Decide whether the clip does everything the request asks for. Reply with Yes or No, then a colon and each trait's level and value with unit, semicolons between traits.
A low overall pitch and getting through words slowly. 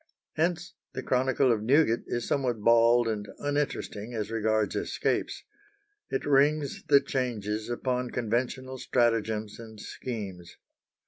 Yes: low, 120 Hz; slow, 120 wpm